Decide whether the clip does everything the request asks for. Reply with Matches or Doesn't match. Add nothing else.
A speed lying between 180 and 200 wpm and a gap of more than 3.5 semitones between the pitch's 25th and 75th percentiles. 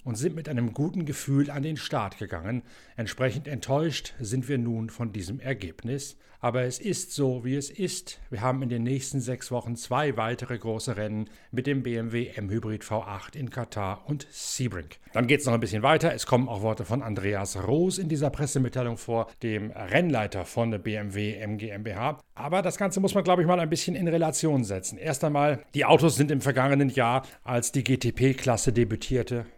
Matches